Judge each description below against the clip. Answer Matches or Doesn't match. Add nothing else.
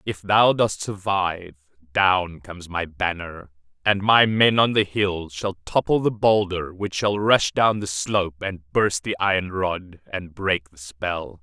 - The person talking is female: Doesn't match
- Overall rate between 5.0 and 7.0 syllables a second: Doesn't match